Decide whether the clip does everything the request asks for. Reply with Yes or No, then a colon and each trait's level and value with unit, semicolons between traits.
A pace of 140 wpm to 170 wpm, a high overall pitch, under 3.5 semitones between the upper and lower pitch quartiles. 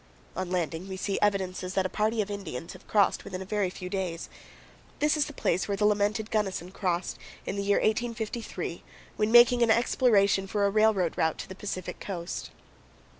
No: average, 190 wpm; high, 200 Hz; average, 2.7 semitones